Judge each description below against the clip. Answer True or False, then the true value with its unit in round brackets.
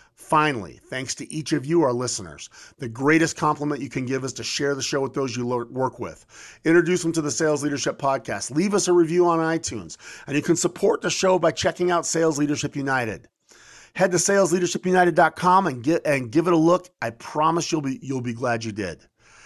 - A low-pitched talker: False (150 Hz)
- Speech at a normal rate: False (215 wpm)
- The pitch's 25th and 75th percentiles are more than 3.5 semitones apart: True (4.7 semitones)